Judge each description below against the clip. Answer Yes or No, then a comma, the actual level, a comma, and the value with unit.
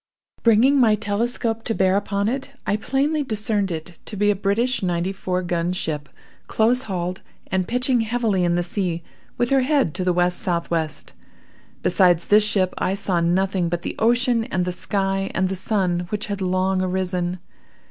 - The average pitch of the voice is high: Yes, high, 195 Hz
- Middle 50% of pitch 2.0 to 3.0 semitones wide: No, average, 3.8 semitones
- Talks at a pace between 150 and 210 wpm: Yes, average, 175 wpm